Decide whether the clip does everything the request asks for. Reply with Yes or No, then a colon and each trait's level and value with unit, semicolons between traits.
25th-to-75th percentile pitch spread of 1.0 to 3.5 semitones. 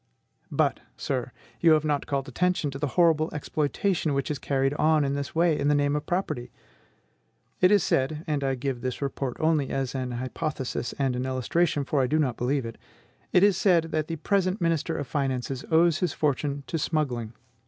Yes: average, 3.2 semitones